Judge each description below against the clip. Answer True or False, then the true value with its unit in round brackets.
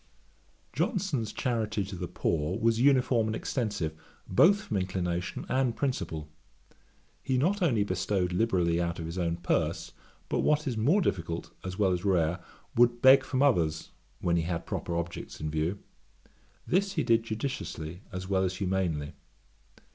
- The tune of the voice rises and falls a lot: True (6.6 semitones)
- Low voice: True (95 Hz)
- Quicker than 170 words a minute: False (155 wpm)